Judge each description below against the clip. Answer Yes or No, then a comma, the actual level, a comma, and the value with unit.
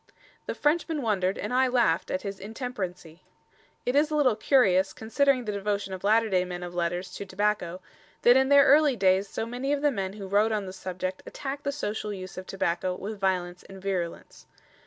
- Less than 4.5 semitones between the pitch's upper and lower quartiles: No, average, 5.2 semitones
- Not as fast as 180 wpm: No, average, 200 wpm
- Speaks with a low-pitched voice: No, high, 205 Hz